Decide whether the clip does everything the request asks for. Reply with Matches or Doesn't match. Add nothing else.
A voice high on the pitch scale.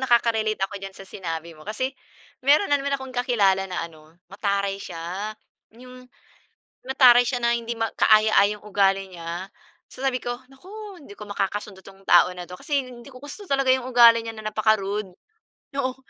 Matches